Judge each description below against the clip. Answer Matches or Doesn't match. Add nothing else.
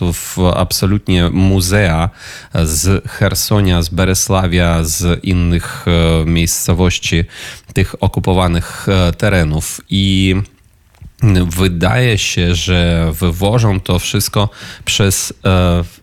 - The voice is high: Doesn't match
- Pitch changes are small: Matches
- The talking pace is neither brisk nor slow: Doesn't match